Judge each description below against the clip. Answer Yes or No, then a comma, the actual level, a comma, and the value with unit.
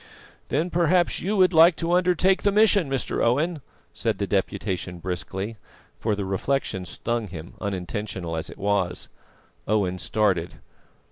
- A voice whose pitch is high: No, low, 110 Hz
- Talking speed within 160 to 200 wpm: No, average, 140 wpm